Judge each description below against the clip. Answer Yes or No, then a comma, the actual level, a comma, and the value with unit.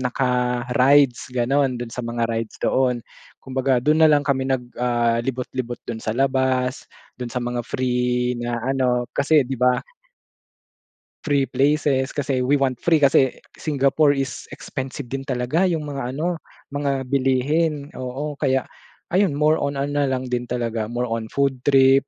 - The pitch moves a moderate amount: No, narrow, 2.3 semitones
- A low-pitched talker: Yes, low, 130 Hz